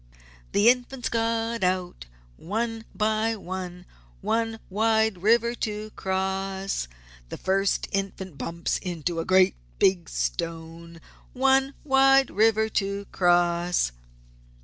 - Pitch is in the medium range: No, high, 195 Hz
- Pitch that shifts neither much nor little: Yes, average, 4.1 semitones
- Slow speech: Yes, slow, 105 wpm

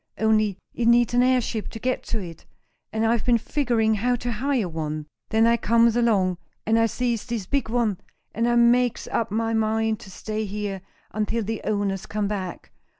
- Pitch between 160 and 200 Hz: No, high, 225 Hz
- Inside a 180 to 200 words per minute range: Yes, average, 190 wpm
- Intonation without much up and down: Yes, narrow, 2.2 semitones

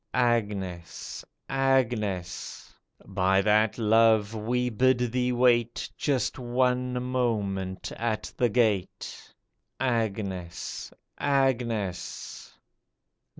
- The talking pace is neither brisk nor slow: No, slow, 75 wpm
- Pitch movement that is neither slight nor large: Yes, average, 3.7 semitones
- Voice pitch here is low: Yes, low, 115 Hz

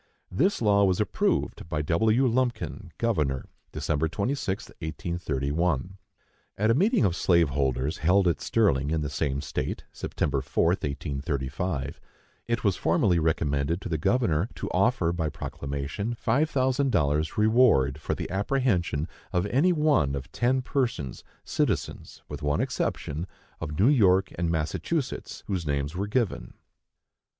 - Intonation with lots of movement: Yes, wide, 7.5 semitones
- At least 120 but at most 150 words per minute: Yes, average, 140 wpm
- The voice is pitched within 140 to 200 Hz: No, very low, 85 Hz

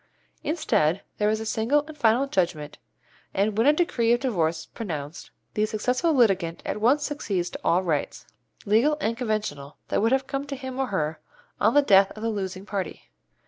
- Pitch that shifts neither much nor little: No, wide, 5.9 semitones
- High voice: Yes, high, 215 Hz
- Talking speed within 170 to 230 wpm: Yes, average, 190 wpm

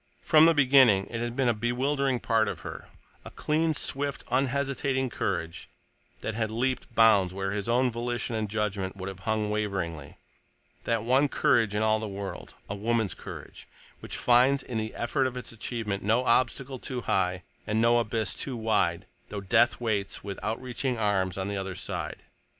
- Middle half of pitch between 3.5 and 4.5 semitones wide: Yes, average, 3.9 semitones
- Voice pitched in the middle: No, low, 115 Hz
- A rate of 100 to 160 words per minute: No, average, 170 wpm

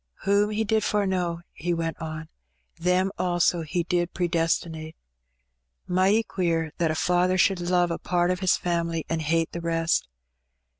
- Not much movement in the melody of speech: Yes, narrow, 1.8 semitones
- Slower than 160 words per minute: No, average, 185 wpm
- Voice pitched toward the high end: No, medium, 175 Hz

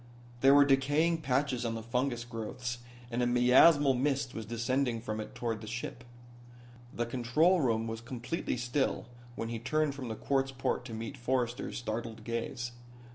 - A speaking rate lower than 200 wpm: Yes, average, 170 wpm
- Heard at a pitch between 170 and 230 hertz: No, low, 125 Hz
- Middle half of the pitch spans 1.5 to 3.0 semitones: Yes, average, 2.7 semitones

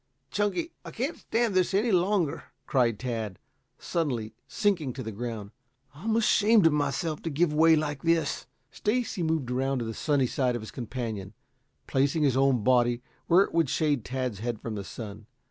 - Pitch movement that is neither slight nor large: No, wide, 6.0 semitones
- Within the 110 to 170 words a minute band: No, average, 180 wpm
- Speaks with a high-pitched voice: No, medium, 140 Hz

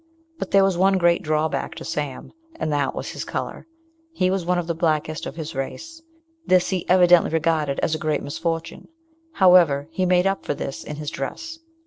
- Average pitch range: Yes, average, 3.2 semitones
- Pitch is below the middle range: No, medium, 165 Hz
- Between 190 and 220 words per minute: Yes, average, 195 wpm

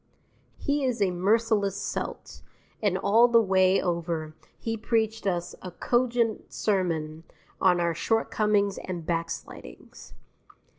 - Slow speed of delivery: Yes, slow, 115 wpm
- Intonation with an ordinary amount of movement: Yes, average, 4.3 semitones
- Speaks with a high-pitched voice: Yes, high, 195 Hz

